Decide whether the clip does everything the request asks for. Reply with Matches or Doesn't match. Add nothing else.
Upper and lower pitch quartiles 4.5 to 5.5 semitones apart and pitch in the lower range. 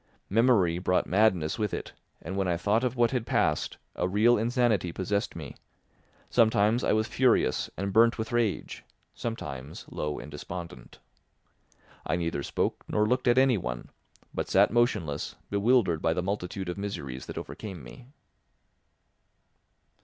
Matches